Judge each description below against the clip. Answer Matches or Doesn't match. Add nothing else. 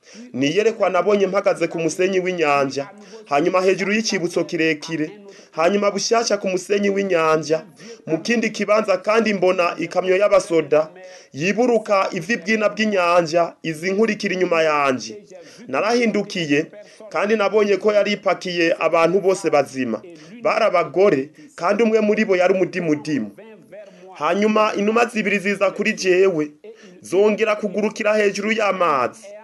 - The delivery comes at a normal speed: Doesn't match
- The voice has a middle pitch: Doesn't match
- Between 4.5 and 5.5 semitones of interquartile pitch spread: Doesn't match